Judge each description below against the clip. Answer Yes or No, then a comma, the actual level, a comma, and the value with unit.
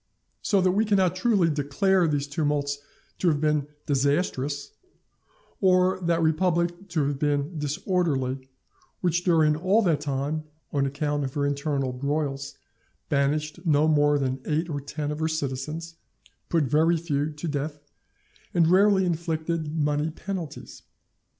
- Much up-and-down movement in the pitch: No, average, 3.2 semitones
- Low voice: No, medium, 155 Hz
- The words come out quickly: No, average, 140 wpm